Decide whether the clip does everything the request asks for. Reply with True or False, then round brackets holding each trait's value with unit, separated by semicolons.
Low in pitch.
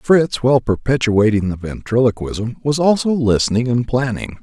True (120 Hz)